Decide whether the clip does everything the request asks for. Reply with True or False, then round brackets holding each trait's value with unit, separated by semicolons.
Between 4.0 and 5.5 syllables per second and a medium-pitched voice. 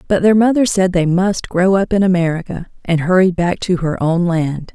True (5.0 syllables/s; 180 Hz)